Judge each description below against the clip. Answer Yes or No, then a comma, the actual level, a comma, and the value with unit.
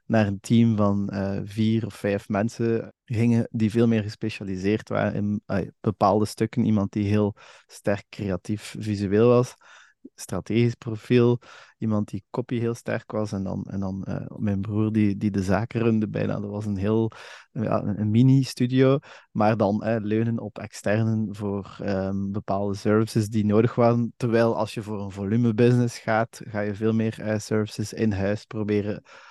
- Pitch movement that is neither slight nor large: No, narrow, 2.1 semitones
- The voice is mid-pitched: No, low, 110 Hz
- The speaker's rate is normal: Yes, average, 170 wpm